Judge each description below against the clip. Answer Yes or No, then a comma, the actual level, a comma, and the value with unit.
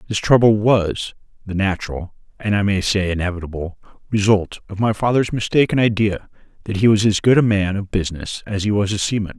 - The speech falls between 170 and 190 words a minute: Yes, average, 180 wpm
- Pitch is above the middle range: No, low, 100 Hz